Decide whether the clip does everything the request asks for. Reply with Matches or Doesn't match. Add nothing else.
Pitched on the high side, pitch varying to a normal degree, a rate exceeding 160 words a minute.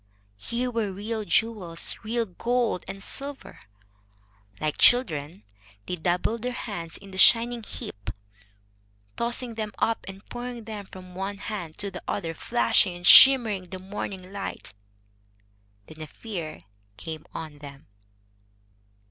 Doesn't match